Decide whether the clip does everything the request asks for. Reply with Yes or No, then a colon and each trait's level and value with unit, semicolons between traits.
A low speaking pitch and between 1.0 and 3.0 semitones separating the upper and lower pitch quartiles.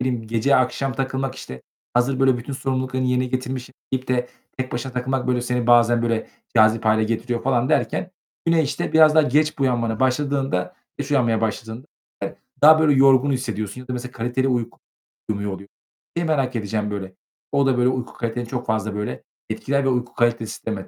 Yes: low, 125 Hz; average, 2.7 semitones